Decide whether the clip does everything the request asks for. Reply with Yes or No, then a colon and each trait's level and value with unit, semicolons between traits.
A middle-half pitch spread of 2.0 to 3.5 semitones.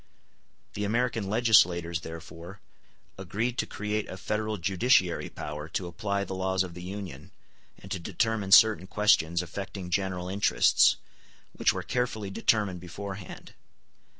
Yes: average, 2.9 semitones